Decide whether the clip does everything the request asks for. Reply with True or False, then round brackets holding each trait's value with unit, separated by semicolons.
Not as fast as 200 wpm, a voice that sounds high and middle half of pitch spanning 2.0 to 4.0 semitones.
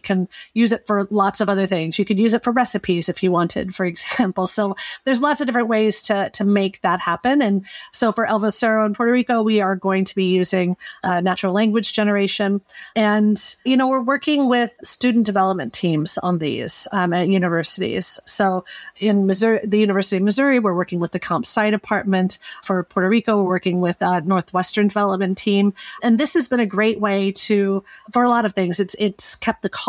False (205 wpm; 205 Hz; 3.1 semitones)